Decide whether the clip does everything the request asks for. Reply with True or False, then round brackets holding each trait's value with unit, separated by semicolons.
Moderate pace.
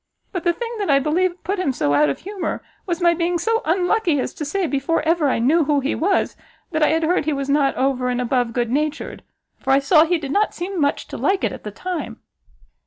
False (245 wpm)